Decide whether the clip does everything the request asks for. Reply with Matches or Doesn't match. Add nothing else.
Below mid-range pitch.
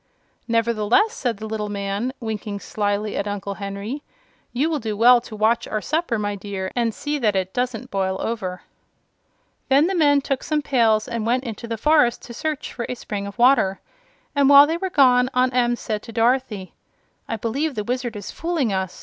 Doesn't match